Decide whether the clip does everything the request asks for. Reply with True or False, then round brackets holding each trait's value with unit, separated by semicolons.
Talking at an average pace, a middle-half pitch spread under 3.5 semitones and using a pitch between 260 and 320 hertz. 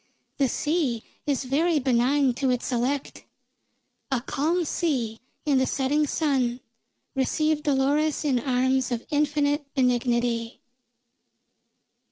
False (110 wpm; 3.0 semitones; 270 Hz)